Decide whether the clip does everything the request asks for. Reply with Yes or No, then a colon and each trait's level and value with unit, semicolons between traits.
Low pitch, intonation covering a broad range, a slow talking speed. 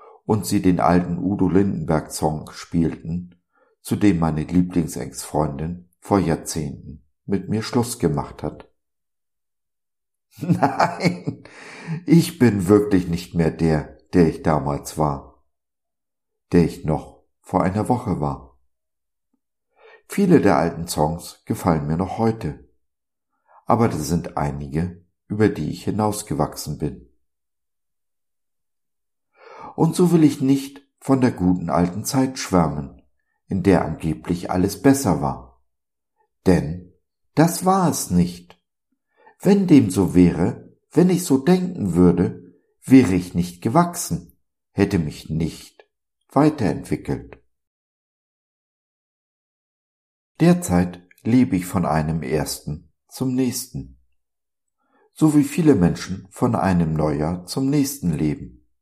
Yes: very low, 90 Hz; wide, 8.4 semitones; slow, 110 wpm